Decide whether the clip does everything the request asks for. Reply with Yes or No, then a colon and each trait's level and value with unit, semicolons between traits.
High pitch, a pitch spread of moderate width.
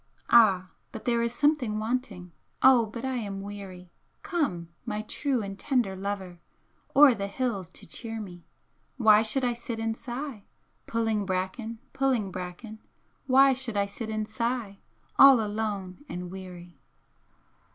Yes: high, 220 Hz; average, 3.9 semitones